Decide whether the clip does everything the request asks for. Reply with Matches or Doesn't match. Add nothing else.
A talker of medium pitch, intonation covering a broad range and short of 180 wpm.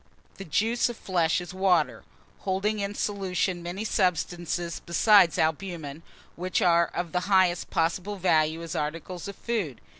Doesn't match